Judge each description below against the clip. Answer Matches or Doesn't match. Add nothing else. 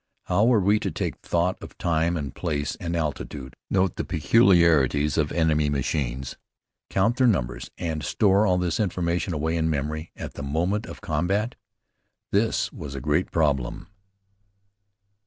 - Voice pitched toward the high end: Doesn't match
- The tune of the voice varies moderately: Matches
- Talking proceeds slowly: Doesn't match